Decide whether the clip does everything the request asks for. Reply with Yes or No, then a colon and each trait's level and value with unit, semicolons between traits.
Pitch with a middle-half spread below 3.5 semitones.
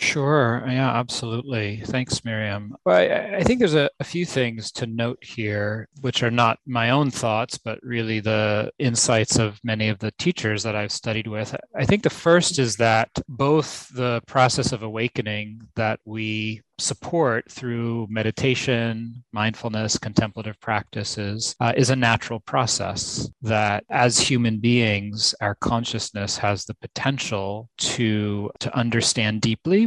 Yes: average, 2.9 semitones